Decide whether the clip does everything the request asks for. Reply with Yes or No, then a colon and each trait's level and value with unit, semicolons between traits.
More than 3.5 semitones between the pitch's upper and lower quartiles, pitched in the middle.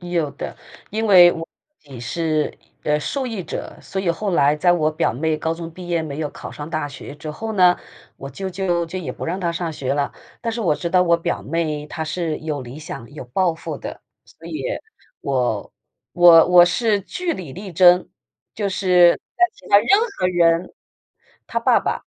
No: average, 3.2 semitones; medium, 170 Hz